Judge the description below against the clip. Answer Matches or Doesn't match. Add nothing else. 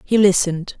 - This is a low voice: Doesn't match